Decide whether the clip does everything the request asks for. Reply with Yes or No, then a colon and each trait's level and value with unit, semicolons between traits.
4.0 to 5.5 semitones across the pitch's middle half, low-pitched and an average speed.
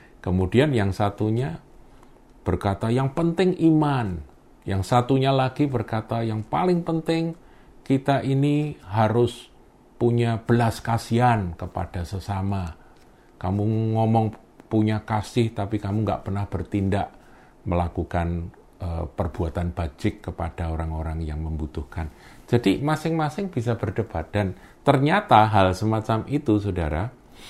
Yes: average, 5.0 semitones; low, 110 Hz; average, 105 wpm